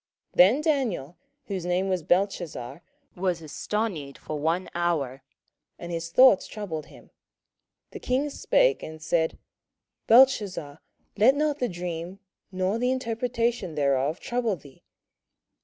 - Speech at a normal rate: No, slow, 125 wpm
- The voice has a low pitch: No, medium, 185 Hz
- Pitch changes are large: Yes, wide, 6.5 semitones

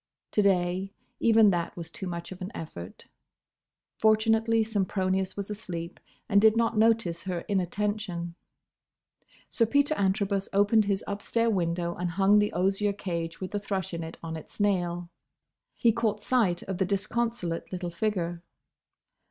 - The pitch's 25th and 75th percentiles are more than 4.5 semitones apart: No, average, 3.4 semitones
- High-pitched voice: Yes, high, 195 Hz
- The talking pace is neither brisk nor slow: Yes, average, 150 wpm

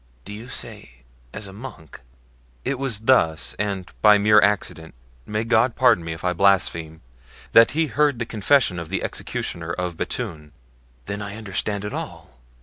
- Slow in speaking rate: No, average, 155 wpm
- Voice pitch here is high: No, low, 100 Hz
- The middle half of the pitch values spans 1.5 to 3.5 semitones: No, average, 5.3 semitones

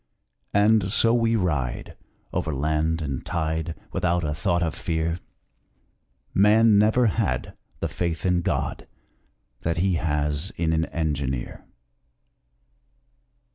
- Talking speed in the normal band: No, slow, 115 wpm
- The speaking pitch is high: No, very low, 85 Hz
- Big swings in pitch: No, average, 3.7 semitones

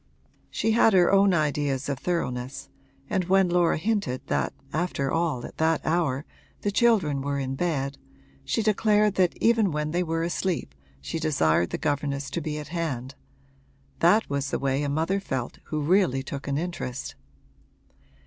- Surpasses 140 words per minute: Yes, average, 165 wpm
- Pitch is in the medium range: Yes, medium, 155 Hz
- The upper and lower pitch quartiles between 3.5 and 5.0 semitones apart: Yes, average, 4.6 semitones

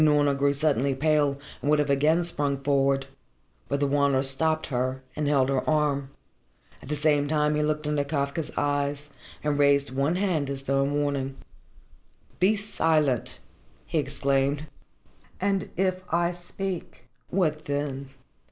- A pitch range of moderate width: No, narrow, 1.9 semitones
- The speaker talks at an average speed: Yes, average, 150 wpm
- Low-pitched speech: No, medium, 145 Hz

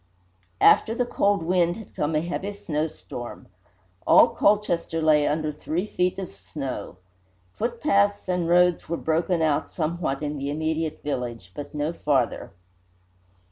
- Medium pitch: Yes, medium, 160 Hz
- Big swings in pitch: No, average, 3.5 semitones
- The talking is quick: No, average, 140 wpm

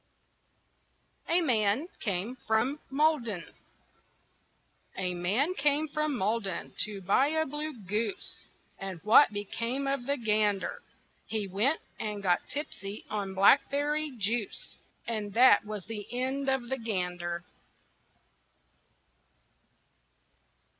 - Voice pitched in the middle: No, high, 225 Hz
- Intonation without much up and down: No, wide, 5.6 semitones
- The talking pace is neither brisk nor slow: No, slow, 105 wpm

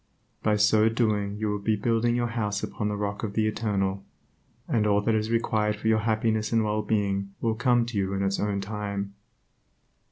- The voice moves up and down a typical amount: No, narrow, 1.6 semitones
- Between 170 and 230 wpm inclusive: Yes, average, 200 wpm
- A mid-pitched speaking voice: No, low, 105 Hz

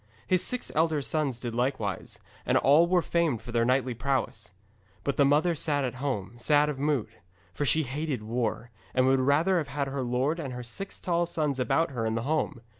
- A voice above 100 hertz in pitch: Yes, medium, 140 Hz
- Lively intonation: No, average, 3.9 semitones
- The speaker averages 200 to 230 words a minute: Yes, fast, 205 wpm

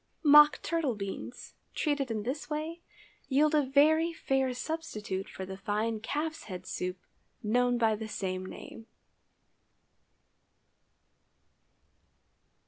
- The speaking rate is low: Yes, slow, 110 wpm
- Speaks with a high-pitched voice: Yes, very high, 250 Hz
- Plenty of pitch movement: Yes, wide, 6.1 semitones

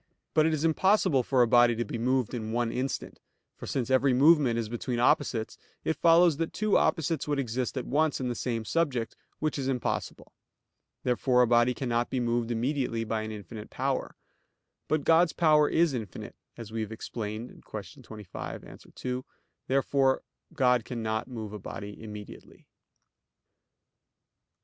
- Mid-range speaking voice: No, low, 125 Hz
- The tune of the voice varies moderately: Yes, average, 3.9 semitones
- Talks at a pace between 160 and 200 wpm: Yes, average, 165 wpm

